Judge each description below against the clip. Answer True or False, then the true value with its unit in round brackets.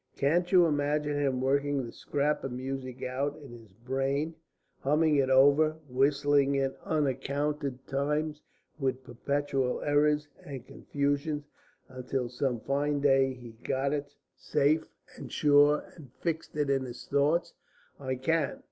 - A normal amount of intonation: False (1.8 semitones)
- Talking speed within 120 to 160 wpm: True (140 wpm)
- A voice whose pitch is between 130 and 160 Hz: True (140 Hz)